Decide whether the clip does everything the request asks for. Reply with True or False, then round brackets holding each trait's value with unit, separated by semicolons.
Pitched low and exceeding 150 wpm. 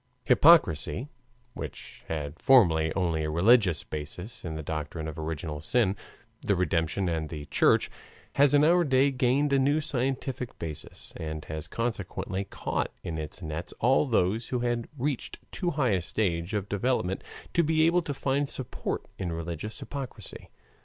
True (100 Hz; 160 wpm)